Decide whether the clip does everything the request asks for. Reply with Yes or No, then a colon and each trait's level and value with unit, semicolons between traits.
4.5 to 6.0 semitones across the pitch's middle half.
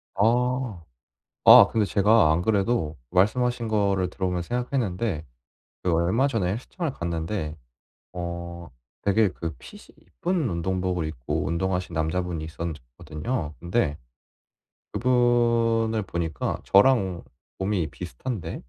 Yes: average, 5.1 semitones